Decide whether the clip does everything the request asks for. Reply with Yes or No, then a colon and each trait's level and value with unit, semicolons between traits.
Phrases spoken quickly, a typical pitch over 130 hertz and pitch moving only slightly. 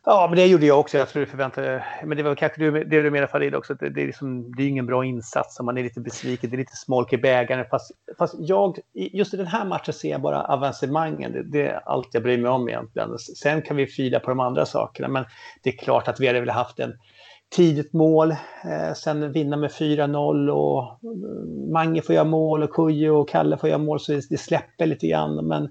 No: fast, 235 wpm; medium, 140 Hz; average, 3.8 semitones